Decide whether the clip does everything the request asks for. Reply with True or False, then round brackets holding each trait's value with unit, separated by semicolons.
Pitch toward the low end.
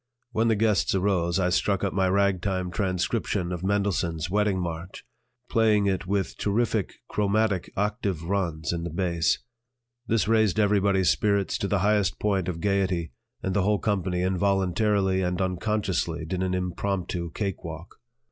True (95 Hz)